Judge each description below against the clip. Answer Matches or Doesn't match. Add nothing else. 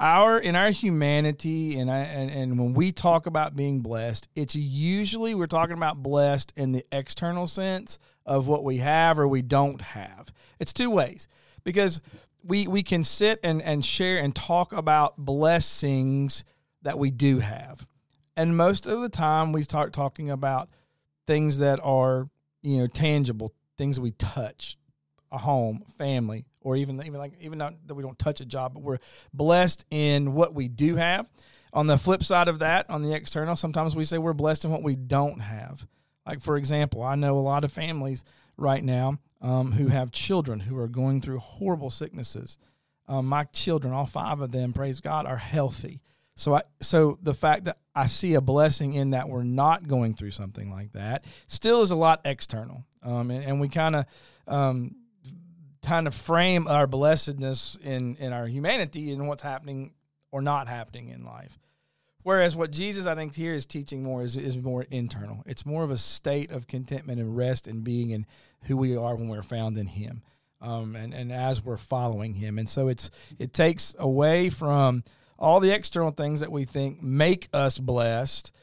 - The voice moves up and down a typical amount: Matches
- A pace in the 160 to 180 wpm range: Doesn't match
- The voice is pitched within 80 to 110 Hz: Doesn't match